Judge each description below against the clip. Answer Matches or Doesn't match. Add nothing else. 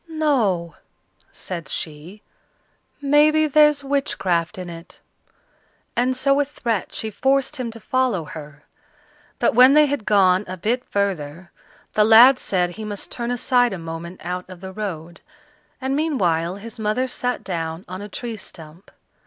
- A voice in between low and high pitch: Doesn't match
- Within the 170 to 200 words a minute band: Doesn't match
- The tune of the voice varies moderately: Doesn't match